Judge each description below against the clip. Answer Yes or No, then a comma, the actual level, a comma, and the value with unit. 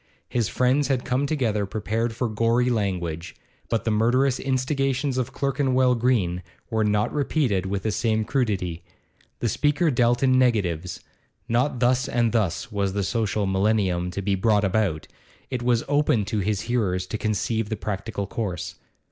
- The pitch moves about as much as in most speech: Yes, average, 4.1 semitones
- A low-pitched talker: Yes, low, 110 Hz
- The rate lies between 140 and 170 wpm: Yes, average, 160 wpm